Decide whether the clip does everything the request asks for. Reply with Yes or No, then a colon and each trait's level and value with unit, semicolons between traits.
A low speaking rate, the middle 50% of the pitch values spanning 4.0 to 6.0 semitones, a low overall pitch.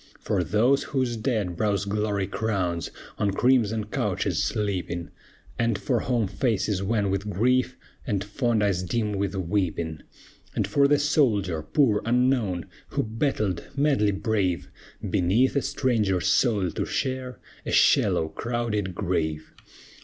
Yes: slow, 130 wpm; average, 4.3 semitones; low, 105 Hz